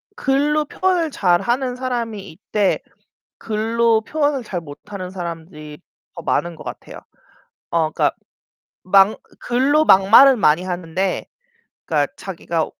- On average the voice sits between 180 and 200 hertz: No, high, 210 Hz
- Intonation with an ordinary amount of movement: No, wide, 6.7 semitones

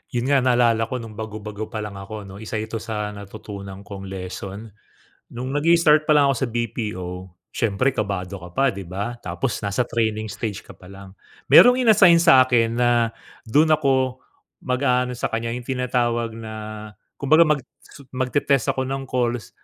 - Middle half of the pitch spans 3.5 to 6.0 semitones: Yes, average, 3.8 semitones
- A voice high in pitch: No, low, 115 Hz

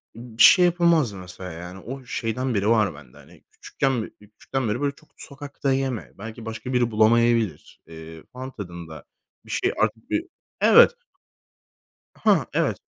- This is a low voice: Yes, low, 115 Hz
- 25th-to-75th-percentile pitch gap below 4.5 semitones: No, average, 5.3 semitones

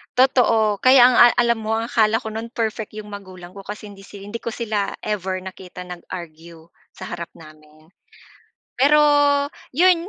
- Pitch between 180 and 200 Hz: No, high, 210 Hz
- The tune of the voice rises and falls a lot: No, average, 4.2 semitones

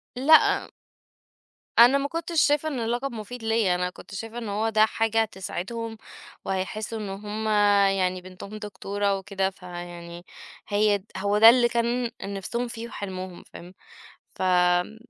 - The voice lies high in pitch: Yes, high, 210 Hz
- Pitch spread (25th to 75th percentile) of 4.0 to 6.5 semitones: No, average, 3.6 semitones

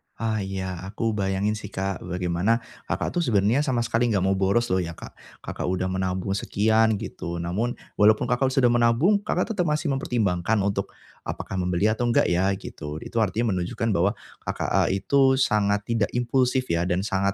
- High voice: No, low, 105 Hz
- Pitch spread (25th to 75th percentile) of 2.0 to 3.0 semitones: No, average, 3.9 semitones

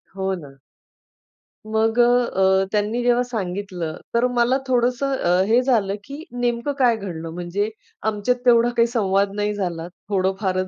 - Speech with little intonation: No, average, 4.1 semitones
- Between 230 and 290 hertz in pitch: No, high, 210 Hz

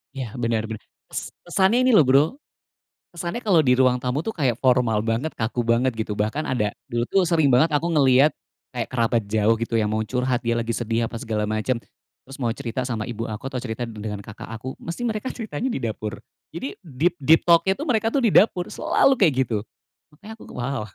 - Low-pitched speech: Yes, low, 125 Hz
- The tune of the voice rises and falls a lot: Yes, wide, 6.1 semitones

